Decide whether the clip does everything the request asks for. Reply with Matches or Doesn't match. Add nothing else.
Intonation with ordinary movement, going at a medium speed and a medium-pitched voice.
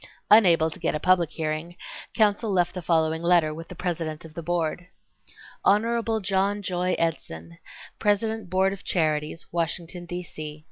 Matches